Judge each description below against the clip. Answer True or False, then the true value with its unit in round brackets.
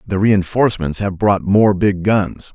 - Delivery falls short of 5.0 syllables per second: True (4.1 syllables/s)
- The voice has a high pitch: False (100 Hz)